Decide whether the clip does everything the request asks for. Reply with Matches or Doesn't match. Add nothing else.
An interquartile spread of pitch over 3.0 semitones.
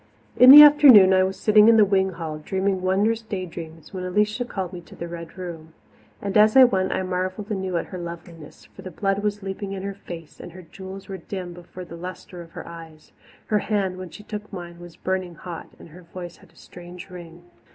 Doesn't match